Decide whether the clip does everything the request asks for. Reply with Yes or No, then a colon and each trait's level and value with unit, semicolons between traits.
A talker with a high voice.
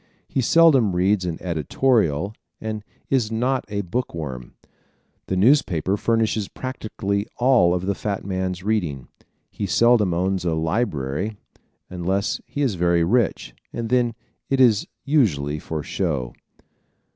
No: low, 100 Hz